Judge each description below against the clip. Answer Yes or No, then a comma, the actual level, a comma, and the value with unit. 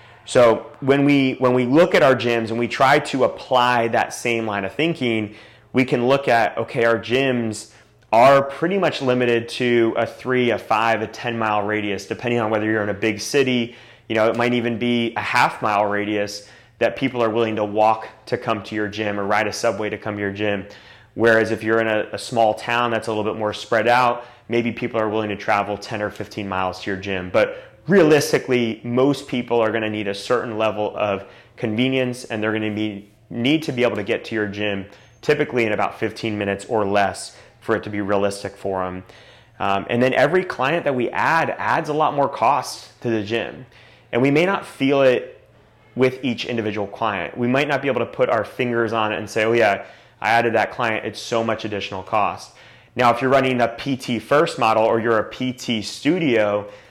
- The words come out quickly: Yes, fast, 220 wpm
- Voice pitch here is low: Yes, low, 115 Hz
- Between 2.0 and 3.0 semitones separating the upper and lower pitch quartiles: Yes, average, 2.7 semitones